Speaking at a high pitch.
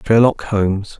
No: low, 105 Hz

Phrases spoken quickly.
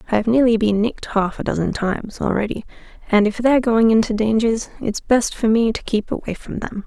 Yes: fast, 210 wpm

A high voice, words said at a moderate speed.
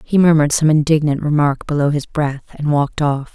No: medium, 150 Hz; average, 195 wpm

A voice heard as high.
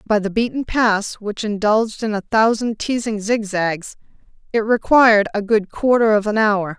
Yes: high, 215 Hz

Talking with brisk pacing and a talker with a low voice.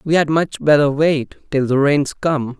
No: fast, 210 wpm; medium, 145 Hz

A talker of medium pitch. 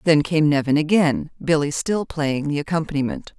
Yes: medium, 155 Hz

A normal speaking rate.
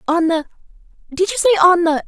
Yes: average, 175 wpm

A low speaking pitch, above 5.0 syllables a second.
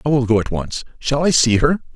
Yes: low, 130 Hz; 5.7 syllables/s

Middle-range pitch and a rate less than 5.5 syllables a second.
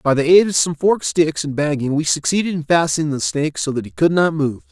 No: medium, 155 Hz; 6.1 syllables/s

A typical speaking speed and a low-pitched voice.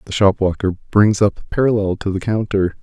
Yes: average, 190 wpm; low, 100 Hz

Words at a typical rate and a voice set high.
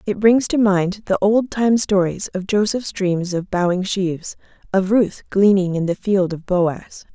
Yes: average, 185 wpm; high, 195 Hz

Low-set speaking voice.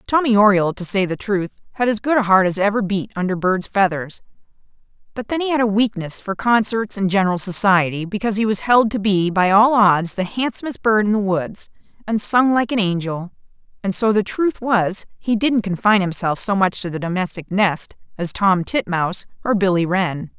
No: high, 200 Hz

